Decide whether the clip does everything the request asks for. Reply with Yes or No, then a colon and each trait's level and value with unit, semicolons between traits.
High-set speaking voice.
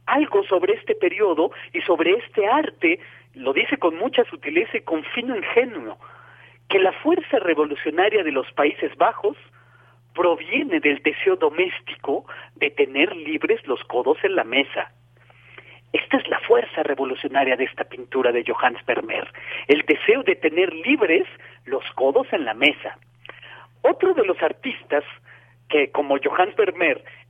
Yes: very high, 290 Hz